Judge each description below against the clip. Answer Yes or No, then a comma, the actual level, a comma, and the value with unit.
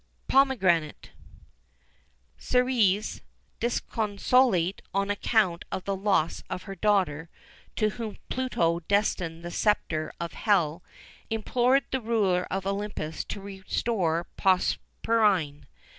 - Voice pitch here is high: Yes, high, 195 Hz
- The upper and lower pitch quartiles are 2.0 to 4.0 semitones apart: No, average, 4.4 semitones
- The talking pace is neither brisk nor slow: No, slow, 100 wpm